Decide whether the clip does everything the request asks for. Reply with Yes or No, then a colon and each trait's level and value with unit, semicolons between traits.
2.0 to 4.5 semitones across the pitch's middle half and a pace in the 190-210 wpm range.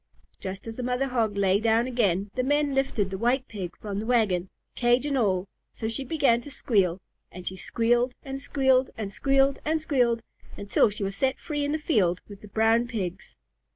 No: average, 4.9 semitones; average, 200 wpm